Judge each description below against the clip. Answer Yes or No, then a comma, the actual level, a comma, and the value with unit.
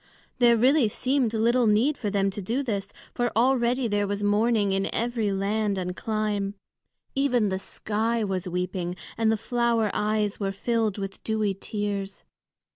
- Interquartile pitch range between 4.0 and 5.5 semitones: No, average, 2.9 semitones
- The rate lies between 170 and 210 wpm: No, average, 160 wpm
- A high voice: Yes, high, 215 Hz